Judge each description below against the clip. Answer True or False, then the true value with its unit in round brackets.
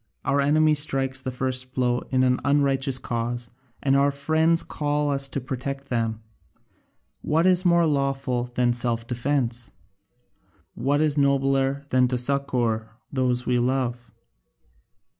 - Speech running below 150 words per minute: True (135 wpm)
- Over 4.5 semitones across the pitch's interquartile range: False (2.4 semitones)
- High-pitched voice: False (135 Hz)